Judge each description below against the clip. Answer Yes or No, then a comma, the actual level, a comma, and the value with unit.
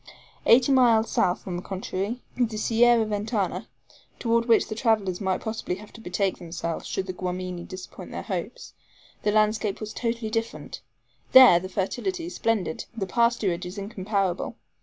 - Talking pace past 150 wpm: Yes, average, 160 wpm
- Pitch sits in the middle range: No, high, 215 Hz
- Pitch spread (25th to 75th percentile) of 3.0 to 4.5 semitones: Yes, average, 3.7 semitones